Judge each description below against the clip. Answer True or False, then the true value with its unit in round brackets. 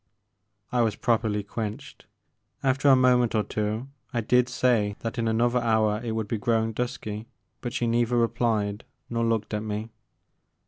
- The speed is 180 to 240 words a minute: False (165 wpm)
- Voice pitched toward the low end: True (115 Hz)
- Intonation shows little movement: True (2.0 semitones)